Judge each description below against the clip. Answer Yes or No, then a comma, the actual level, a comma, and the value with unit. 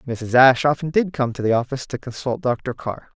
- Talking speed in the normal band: No, fast, 225 wpm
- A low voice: Yes, low, 130 Hz